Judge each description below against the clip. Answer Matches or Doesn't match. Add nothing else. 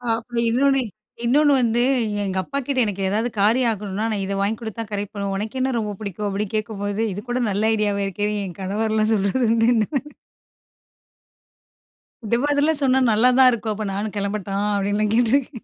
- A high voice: Matches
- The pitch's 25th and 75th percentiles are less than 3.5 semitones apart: Matches